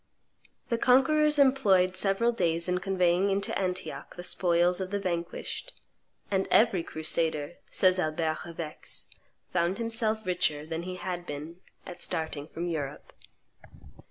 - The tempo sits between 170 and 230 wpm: No, slow, 135 wpm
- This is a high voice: No, medium, 180 Hz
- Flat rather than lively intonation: No, average, 3.0 semitones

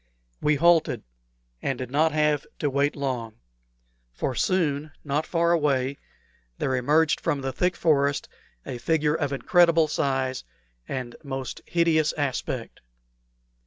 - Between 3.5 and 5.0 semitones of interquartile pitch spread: No, average, 3.1 semitones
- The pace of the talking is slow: Yes, slow, 125 wpm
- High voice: No, medium, 145 Hz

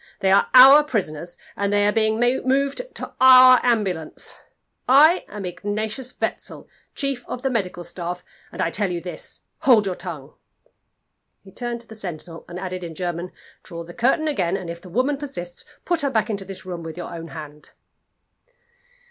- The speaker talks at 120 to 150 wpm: No, average, 180 wpm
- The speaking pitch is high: Yes, high, 200 Hz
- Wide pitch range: Yes, wide, 6.3 semitones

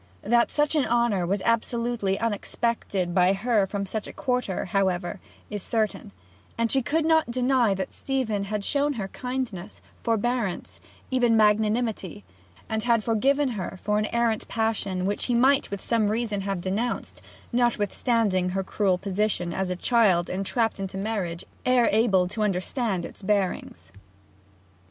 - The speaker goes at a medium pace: Yes, average, 145 wpm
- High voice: Yes, high, 215 Hz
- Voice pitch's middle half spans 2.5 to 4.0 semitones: Yes, average, 3.7 semitones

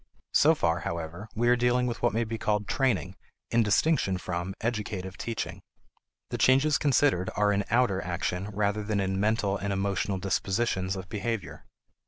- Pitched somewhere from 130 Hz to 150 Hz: No, low, 105 Hz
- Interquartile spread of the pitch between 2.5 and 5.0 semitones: Yes, average, 3.7 semitones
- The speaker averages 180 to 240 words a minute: No, average, 165 wpm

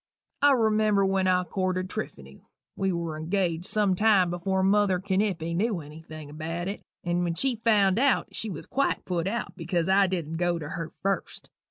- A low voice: No, medium, 185 Hz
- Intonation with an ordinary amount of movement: Yes, average, 3.3 semitones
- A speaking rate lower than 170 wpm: No, average, 185 wpm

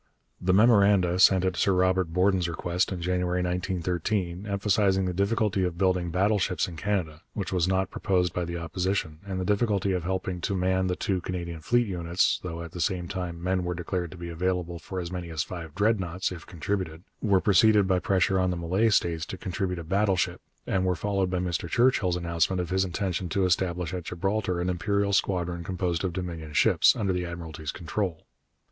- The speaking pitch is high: No, very low, 90 Hz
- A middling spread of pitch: No, narrow, 1.9 semitones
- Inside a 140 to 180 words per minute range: No, average, 195 wpm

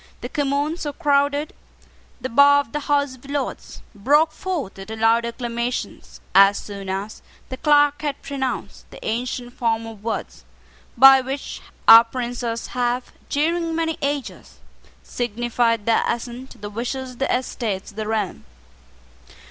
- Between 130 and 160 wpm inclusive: Yes, average, 150 wpm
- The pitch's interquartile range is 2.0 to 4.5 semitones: Yes, average, 3.8 semitones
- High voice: Yes, very high, 250 Hz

